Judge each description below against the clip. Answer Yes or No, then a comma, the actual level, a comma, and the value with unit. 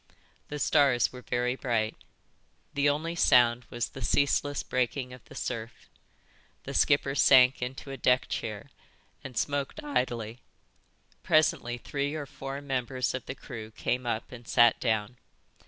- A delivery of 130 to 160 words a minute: Yes, average, 145 wpm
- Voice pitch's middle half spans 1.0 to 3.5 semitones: Yes, average, 2.7 semitones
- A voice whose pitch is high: No, low, 125 Hz